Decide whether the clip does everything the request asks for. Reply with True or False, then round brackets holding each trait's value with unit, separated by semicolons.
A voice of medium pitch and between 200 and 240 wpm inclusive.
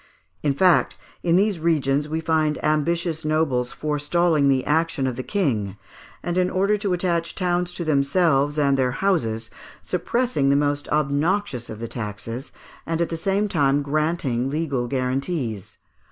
False (150 Hz; 155 wpm)